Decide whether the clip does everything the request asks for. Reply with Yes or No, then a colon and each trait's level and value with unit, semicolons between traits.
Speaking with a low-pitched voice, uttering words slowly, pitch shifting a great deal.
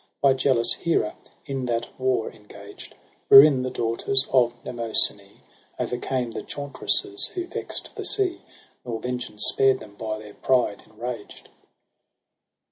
No: low, 125 Hz; slow, 125 wpm; average, 3.0 semitones